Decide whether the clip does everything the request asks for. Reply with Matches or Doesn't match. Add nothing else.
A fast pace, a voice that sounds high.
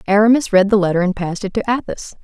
Matches